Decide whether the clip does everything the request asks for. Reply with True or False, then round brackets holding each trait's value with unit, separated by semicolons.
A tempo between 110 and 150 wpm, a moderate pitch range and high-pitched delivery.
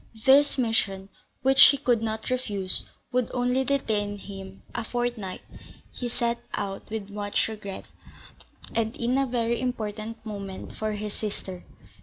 True (140 wpm; 3.2 semitones; 220 Hz)